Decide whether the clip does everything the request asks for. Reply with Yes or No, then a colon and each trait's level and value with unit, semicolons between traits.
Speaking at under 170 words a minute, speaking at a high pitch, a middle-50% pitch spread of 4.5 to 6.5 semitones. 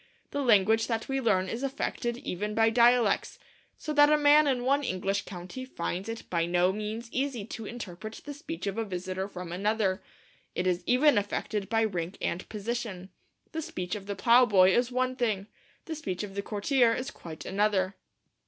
No: average, 190 wpm; high, 215 Hz; average, 4.8 semitones